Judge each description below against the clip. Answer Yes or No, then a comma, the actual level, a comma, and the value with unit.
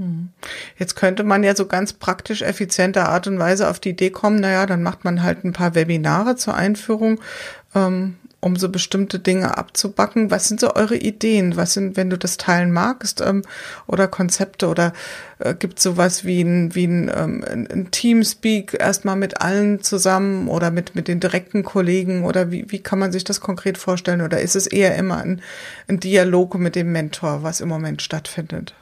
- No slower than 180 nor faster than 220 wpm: Yes, fast, 190 wpm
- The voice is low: No, high, 190 Hz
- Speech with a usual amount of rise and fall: No, narrow, 2.0 semitones